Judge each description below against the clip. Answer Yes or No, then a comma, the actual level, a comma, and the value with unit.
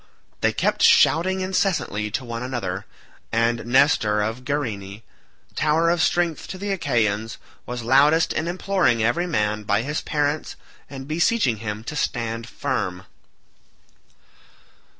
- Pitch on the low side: Yes, low, 125 Hz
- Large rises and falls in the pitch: Yes, wide, 6.4 semitones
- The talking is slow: Yes, slow, 130 wpm